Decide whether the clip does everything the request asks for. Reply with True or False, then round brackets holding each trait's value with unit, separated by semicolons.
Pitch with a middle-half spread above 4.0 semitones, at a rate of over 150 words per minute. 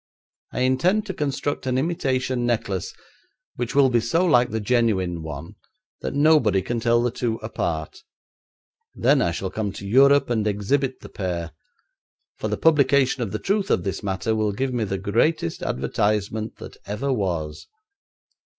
True (5.2 semitones; 160 wpm)